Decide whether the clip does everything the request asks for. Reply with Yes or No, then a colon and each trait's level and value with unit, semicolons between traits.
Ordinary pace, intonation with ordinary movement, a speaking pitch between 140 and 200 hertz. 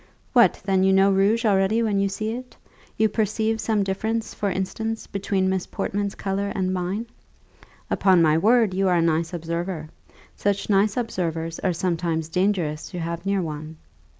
Yes: average, 170 wpm; average, 3.3 semitones; high, 190 Hz